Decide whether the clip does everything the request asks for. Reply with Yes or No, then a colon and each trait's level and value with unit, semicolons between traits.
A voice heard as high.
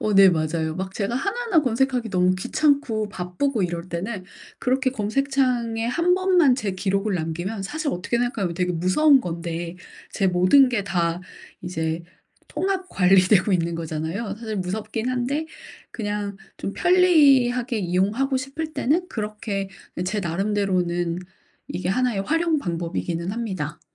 Yes: high, 205 Hz